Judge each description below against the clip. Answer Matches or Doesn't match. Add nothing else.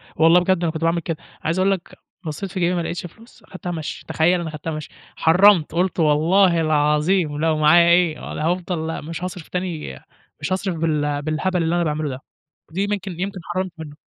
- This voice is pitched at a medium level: Matches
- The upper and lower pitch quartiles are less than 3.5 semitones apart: Matches